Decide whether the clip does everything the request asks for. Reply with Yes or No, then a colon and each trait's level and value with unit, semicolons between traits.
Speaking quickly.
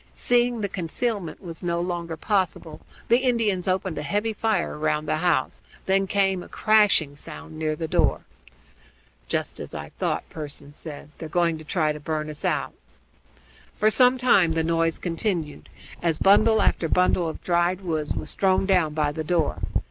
No: average, 170 wpm